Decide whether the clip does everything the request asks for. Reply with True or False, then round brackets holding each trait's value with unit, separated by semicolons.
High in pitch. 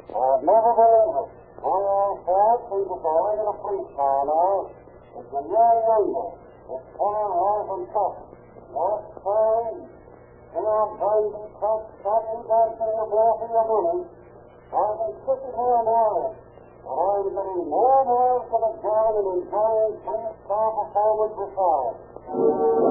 True (215 Hz)